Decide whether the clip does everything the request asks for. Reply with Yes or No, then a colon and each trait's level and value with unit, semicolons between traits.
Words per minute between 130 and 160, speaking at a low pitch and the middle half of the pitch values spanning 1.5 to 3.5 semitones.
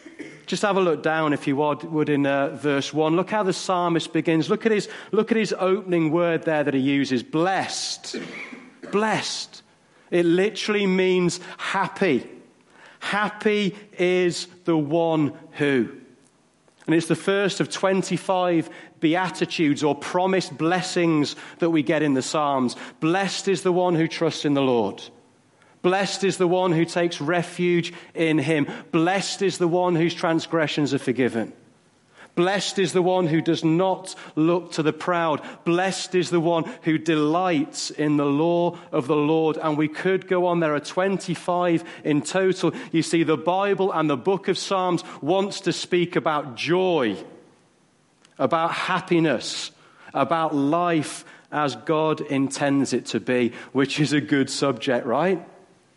No: average, 155 wpm; medium, 170 Hz; average, 3.2 semitones